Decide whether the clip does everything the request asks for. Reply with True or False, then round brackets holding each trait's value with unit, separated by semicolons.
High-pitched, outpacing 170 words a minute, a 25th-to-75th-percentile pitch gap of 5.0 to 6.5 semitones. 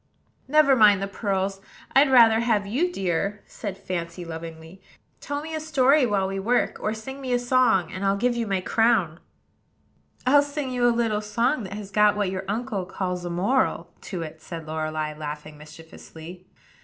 True (200 Hz; 180 wpm; 5.6 semitones)